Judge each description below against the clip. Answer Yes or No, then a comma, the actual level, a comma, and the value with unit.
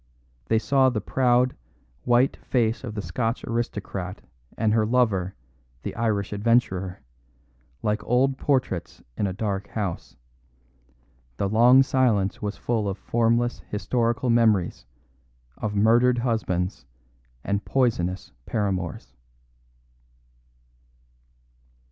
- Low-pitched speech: Yes, low, 110 Hz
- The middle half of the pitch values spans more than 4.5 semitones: No, average, 3.3 semitones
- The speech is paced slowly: Yes, slow, 105 wpm